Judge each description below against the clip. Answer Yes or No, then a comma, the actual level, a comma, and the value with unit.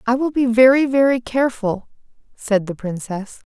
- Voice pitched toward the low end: No, high, 240 Hz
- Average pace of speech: Yes, average, 150 wpm